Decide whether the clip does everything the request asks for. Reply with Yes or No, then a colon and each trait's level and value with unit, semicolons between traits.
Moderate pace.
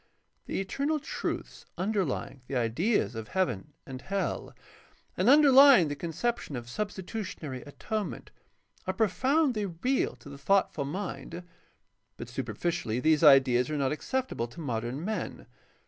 No: slow, 130 wpm